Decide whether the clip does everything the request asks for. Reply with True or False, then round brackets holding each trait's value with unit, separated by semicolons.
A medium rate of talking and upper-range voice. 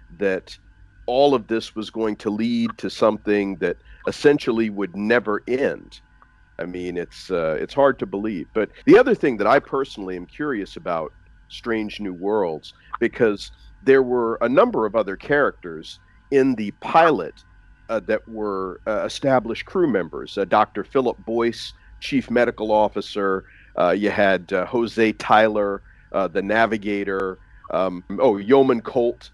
False (150 wpm; 105 Hz)